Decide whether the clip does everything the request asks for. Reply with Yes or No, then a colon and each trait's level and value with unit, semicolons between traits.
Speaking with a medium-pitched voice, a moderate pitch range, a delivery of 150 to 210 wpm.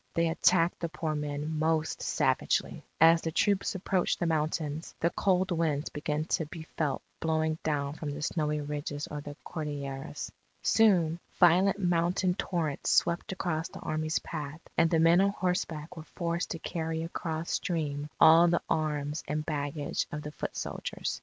No: medium, 160 Hz; narrow, 2.2 semitones; average, 165 wpm